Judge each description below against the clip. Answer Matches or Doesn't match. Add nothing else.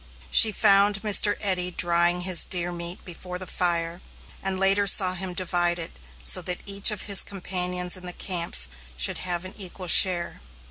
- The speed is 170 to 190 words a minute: Matches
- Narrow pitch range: Matches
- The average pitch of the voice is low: Doesn't match